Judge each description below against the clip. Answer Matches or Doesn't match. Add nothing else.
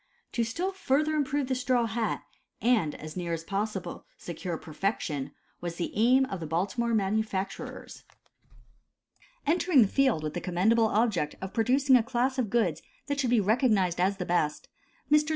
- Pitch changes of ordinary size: Doesn't match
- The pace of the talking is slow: Doesn't match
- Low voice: Doesn't match